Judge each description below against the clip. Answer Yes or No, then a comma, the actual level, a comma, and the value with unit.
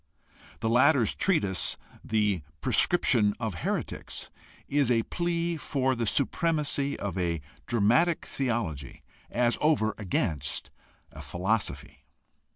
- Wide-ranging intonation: Yes, wide, 6.2 semitones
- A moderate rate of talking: No, slow, 105 wpm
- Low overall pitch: Yes, low, 115 Hz